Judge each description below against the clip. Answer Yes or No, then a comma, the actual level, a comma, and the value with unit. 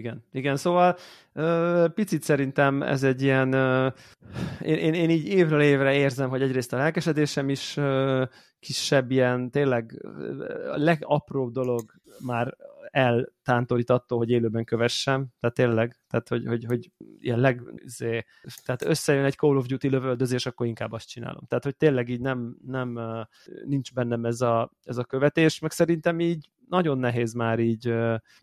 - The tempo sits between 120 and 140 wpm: No, average, 150 wpm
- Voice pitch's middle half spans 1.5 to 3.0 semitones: No, average, 3.5 semitones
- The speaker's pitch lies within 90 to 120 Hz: No, low, 130 Hz